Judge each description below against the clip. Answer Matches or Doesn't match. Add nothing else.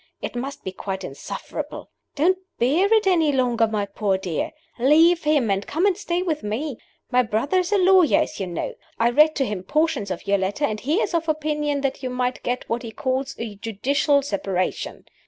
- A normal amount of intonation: Doesn't match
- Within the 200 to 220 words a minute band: Matches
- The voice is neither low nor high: Doesn't match